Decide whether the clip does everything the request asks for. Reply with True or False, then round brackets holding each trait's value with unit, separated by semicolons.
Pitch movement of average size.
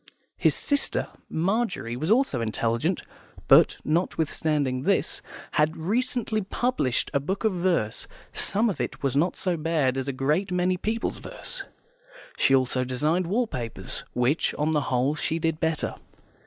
False (5.9 semitones)